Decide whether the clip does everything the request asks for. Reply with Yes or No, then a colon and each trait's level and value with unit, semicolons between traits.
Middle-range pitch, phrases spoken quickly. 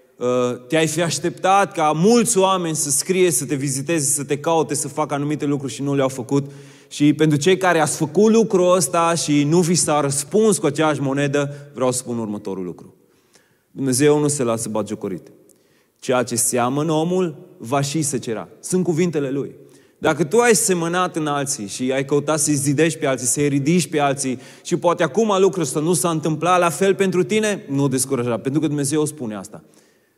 Yes: medium, 150 Hz; fast, 190 wpm